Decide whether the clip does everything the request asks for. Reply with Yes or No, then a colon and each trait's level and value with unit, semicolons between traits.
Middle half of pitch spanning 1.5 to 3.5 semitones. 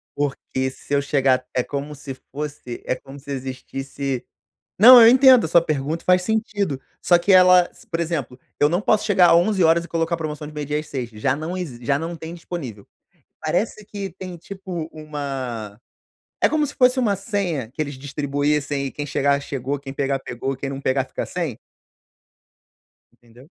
No: average, 4.7 semitones